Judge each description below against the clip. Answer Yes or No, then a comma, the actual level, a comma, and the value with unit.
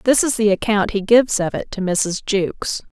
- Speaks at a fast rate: Yes, fast, 225 wpm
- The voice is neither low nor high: No, high, 210 Hz